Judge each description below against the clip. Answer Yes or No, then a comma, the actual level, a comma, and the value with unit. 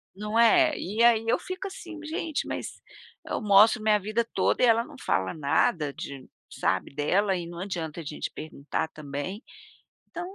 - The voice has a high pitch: Yes, high, 205 Hz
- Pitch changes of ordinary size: No, wide, 6.7 semitones